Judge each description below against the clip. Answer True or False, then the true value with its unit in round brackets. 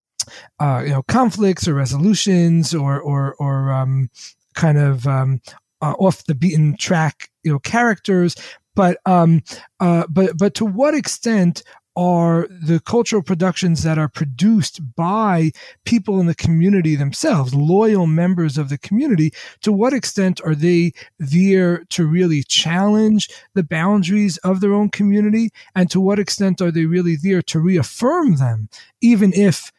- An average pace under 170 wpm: True (150 wpm)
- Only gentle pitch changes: False (4.2 semitones)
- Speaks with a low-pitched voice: False (175 Hz)